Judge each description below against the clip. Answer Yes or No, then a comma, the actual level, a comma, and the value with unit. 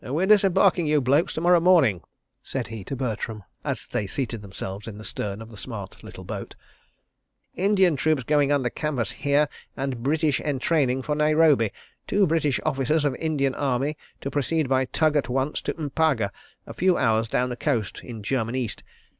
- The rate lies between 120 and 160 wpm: No, average, 180 wpm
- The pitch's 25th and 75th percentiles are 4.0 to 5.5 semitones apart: Yes, average, 4.8 semitones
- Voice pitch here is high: No, medium, 140 Hz